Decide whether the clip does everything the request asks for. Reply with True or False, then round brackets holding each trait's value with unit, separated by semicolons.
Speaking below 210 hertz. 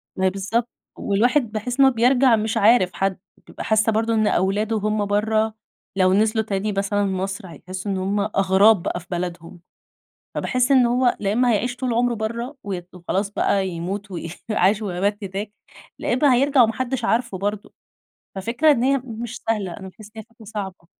False (215 Hz)